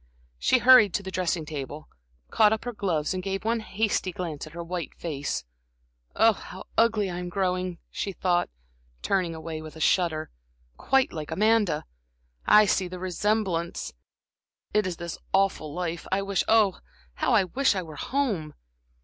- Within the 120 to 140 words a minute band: No, average, 165 wpm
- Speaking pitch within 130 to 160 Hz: No, medium, 185 Hz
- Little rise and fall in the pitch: No, average, 4.0 semitones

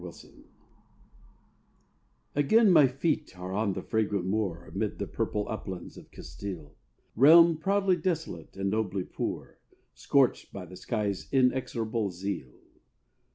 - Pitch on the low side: Yes, low, 110 Hz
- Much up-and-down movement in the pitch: Yes, wide, 6.9 semitones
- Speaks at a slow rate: Yes, slow, 120 wpm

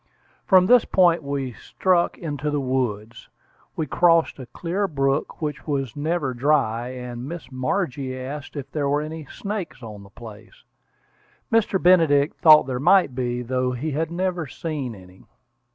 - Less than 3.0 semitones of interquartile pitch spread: No, average, 4.6 semitones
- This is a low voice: No, medium, 145 Hz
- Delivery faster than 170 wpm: No, average, 155 wpm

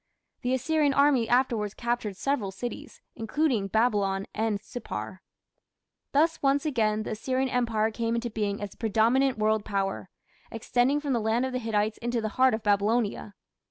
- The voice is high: Yes, high, 230 Hz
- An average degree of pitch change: Yes, average, 3.4 semitones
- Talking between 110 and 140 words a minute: No, average, 160 wpm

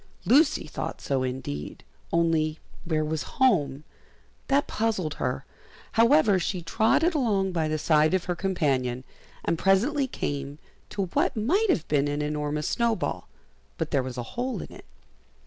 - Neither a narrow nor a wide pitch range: No, wide, 7.4 semitones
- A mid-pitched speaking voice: Yes, medium, 165 Hz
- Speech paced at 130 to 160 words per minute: Yes, average, 150 wpm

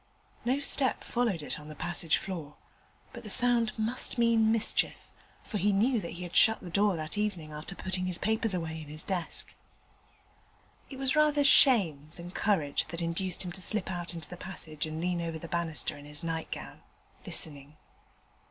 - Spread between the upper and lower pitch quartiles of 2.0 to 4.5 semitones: No, average, 5.3 semitones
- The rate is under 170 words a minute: No, average, 185 wpm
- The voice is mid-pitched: Yes, medium, 180 Hz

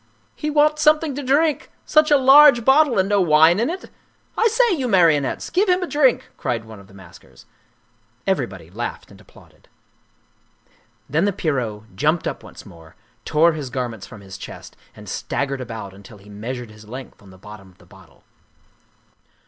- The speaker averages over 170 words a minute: Yes, average, 180 wpm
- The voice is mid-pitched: Yes, medium, 155 Hz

